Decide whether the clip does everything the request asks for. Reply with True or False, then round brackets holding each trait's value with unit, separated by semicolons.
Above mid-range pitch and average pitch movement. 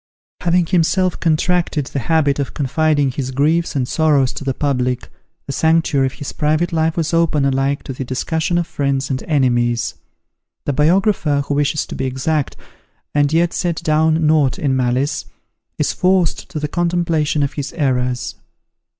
False (150 Hz; 3.2 semitones)